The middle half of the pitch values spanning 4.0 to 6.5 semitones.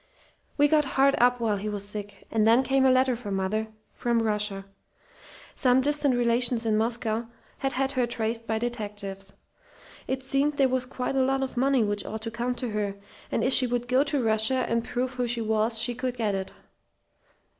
No: average, 3.0 semitones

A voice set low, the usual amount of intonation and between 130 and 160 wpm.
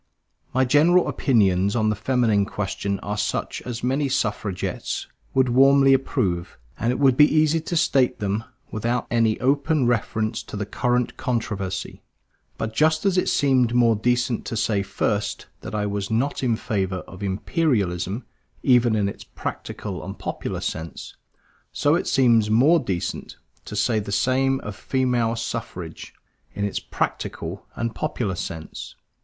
Yes: low, 115 Hz; average, 4.5 semitones; average, 150 wpm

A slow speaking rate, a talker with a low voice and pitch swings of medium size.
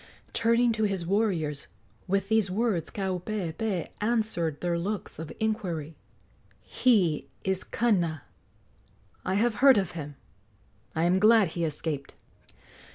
No: slow, 120 wpm; high, 190 Hz; average, 4.7 semitones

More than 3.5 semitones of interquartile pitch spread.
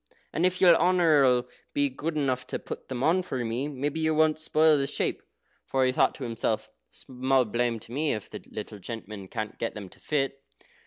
Yes: average, 4.5 semitones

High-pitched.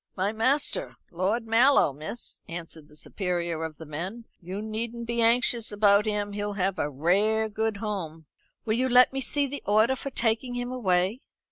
Yes: high, 215 Hz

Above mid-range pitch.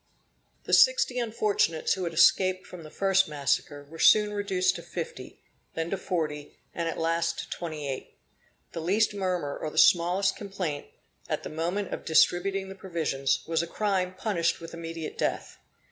No: medium, 175 Hz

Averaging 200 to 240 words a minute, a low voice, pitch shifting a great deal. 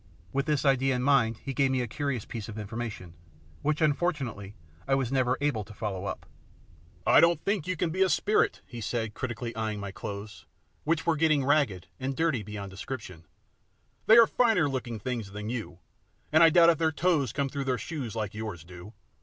Yes: fast, 205 wpm; low, 130 Hz; wide, 6.0 semitones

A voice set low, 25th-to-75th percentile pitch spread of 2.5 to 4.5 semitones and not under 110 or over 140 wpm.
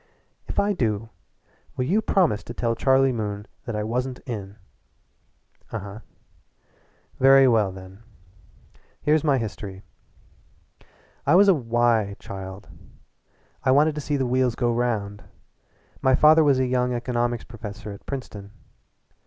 Yes: low, 120 Hz; average, 4.2 semitones; slow, 135 wpm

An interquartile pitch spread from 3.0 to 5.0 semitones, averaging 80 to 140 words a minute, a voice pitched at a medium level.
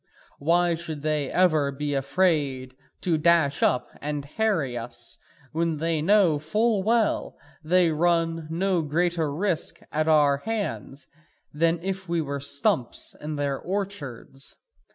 Yes: average, 3.6 semitones; slow, 135 wpm; medium, 160 Hz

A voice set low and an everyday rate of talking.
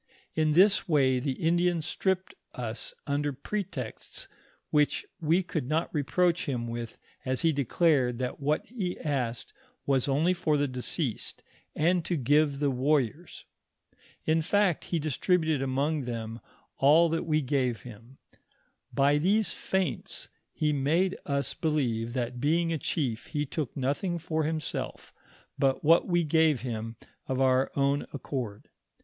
No: medium, 145 Hz; average, 145 wpm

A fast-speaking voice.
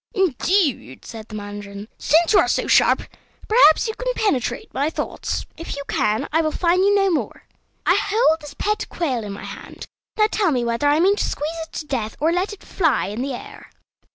Yes: fast, 215 wpm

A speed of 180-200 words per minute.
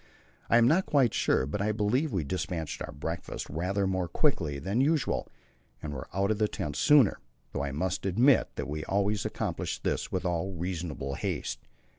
Yes: average, 185 wpm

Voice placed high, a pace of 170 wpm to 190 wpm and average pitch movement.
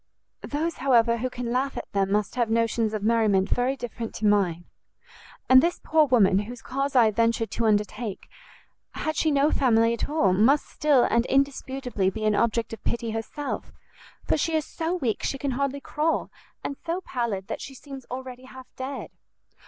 Yes: high, 245 Hz; average, 185 wpm; average, 3.8 semitones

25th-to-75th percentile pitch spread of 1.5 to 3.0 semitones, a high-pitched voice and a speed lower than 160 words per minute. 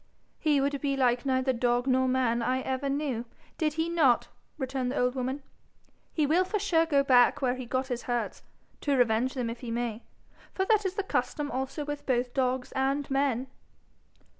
No: narrow, 2.6 semitones; very high, 260 Hz; average, 190 wpm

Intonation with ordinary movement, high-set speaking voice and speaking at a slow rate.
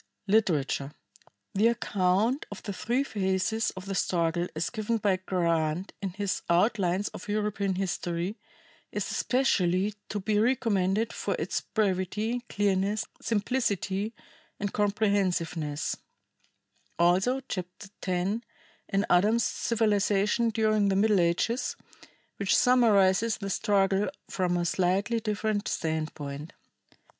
Yes: average, 3.0 semitones; high, 200 Hz; slow, 115 wpm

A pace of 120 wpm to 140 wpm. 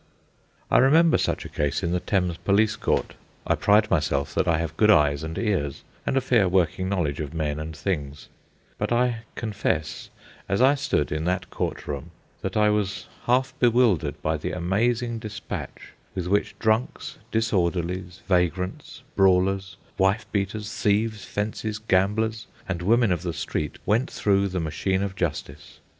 No: average, 160 wpm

